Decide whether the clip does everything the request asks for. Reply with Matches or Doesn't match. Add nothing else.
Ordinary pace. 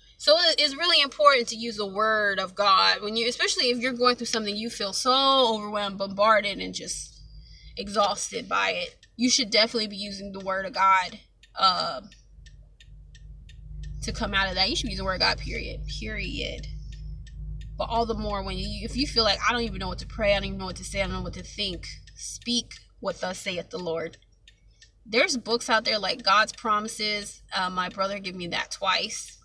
Doesn't match